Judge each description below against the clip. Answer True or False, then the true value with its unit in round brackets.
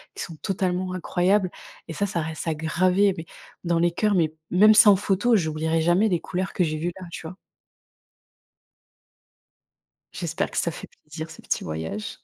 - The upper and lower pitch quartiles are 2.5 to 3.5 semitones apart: True (3.0 semitones)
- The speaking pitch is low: False (175 Hz)